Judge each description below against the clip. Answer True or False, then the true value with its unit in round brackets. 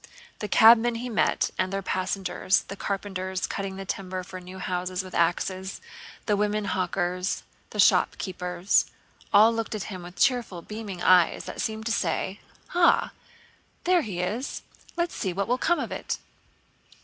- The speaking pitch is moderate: False (195 Hz)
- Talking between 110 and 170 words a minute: True (160 wpm)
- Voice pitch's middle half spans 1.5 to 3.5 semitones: True (3.0 semitones)